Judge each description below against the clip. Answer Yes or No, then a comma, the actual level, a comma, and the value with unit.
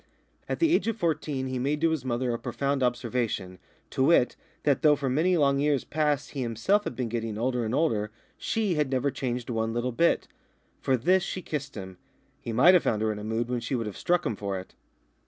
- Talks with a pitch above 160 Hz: No, low, 130 Hz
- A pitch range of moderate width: Yes, average, 4.5 semitones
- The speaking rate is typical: No, fast, 230 wpm